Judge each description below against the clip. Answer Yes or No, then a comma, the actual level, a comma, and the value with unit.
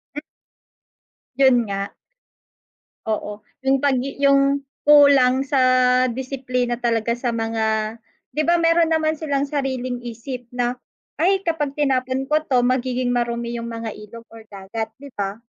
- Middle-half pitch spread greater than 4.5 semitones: No, average, 3.2 semitones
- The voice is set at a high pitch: Yes, very high, 255 Hz